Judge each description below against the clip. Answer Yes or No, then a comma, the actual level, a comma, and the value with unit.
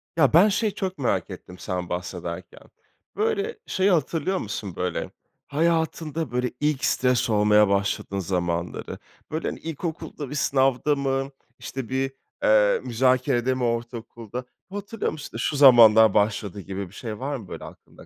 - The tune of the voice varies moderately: No, wide, 6.5 semitones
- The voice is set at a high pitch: No, low, 125 Hz